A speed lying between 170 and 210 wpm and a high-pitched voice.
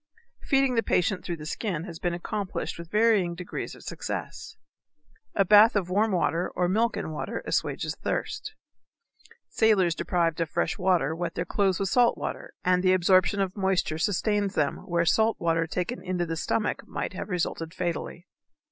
No: average, 175 wpm; medium, 180 Hz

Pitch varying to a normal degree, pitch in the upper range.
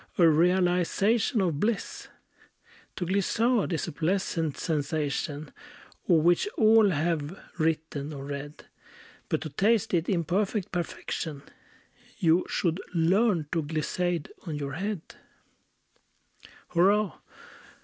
No: average, 4.0 semitones; medium, 170 Hz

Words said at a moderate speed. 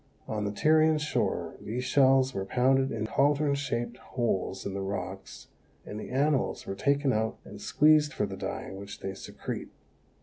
Yes: average, 170 wpm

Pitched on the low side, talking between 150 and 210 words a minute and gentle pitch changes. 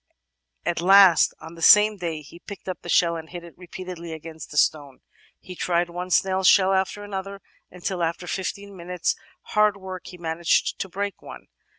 No: medium, 180 Hz; average, 185 wpm; narrow, 2.2 semitones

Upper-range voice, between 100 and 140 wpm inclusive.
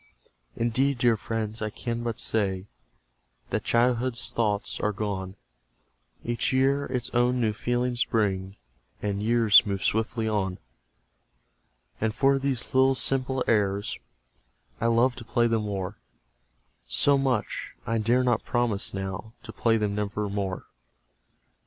No: low, 115 Hz; slow, 135 wpm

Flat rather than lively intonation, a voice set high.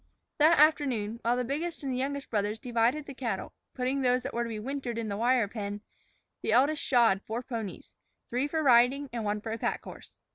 No: average, 3.6 semitones; high, 245 Hz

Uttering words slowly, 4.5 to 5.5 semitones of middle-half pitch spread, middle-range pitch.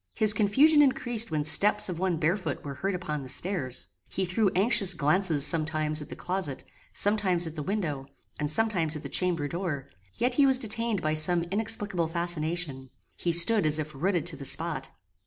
No: average, 185 wpm; average, 4.8 semitones; medium, 170 Hz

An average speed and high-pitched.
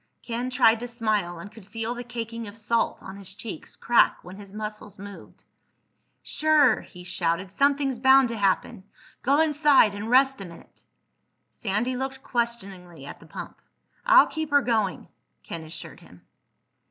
Yes: average, 160 wpm; high, 225 Hz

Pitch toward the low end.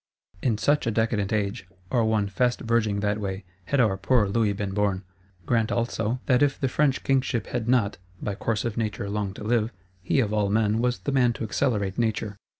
Yes: low, 110 Hz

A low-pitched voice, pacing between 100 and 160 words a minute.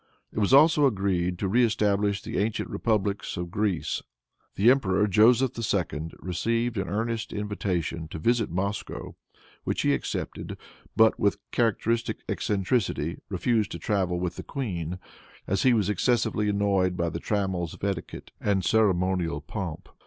Yes: low, 100 Hz; average, 145 wpm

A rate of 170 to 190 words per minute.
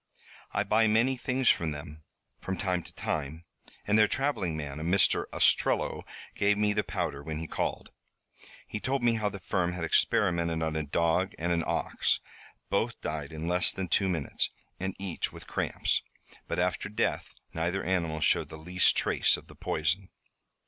Yes: average, 175 wpm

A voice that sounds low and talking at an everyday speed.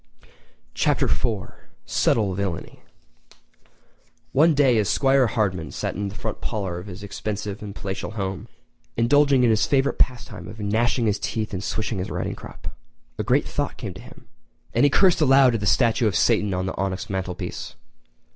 Yes: low, 105 Hz; average, 175 wpm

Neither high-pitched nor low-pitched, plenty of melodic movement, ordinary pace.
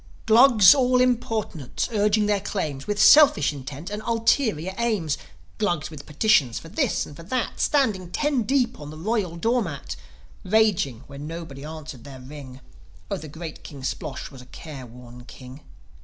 Yes: medium, 170 Hz; wide, 7.5 semitones; average, 160 wpm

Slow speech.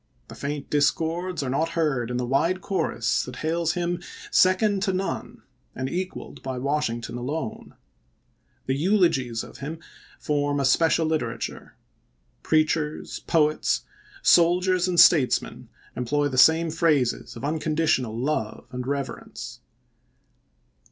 Yes: slow, 125 wpm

